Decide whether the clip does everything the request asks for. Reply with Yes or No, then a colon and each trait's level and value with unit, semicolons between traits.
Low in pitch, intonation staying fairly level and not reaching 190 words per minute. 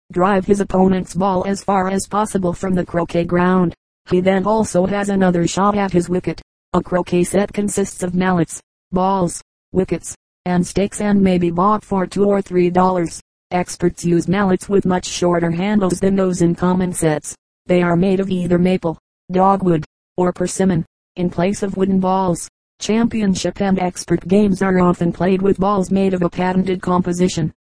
No: medium, 185 Hz; narrow, 1.7 semitones; average, 175 wpm